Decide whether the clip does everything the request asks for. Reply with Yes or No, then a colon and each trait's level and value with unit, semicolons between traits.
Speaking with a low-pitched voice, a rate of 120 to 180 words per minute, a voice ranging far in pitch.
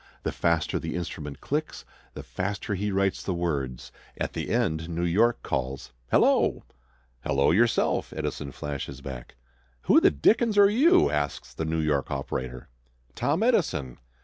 Yes: very low, 85 Hz; average, 150 wpm; wide, 8.6 semitones